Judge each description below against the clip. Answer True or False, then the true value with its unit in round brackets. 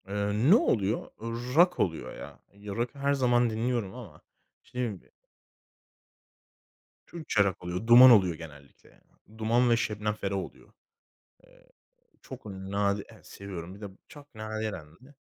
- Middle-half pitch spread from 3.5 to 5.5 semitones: True (3.9 semitones)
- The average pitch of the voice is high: False (110 Hz)